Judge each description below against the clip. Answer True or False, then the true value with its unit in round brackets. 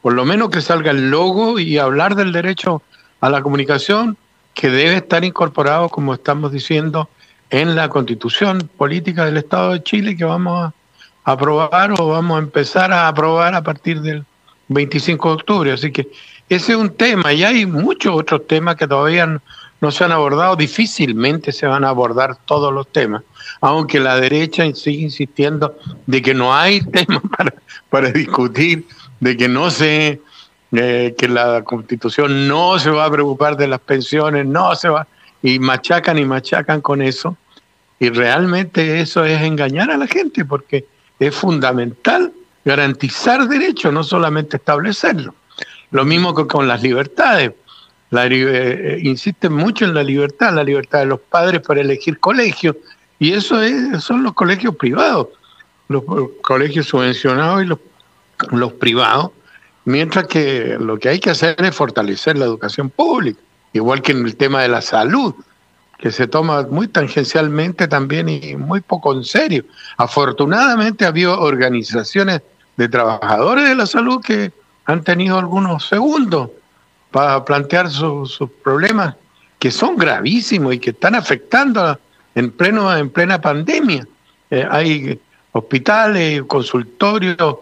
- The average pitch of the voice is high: False (155 Hz)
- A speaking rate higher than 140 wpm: True (155 wpm)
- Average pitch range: True (4.7 semitones)